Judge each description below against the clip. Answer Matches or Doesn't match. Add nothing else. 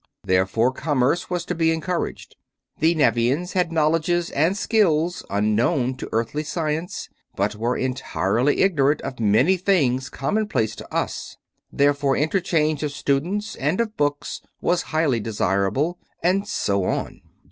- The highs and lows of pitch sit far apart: Matches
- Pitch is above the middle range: Doesn't match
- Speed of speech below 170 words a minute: Matches